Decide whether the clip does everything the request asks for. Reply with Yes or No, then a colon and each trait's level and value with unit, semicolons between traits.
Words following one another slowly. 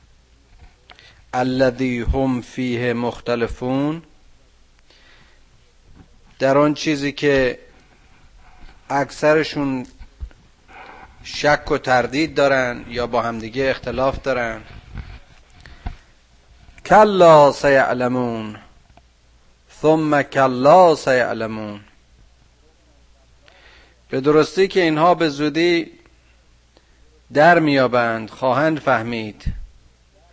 Yes: slow, 65 wpm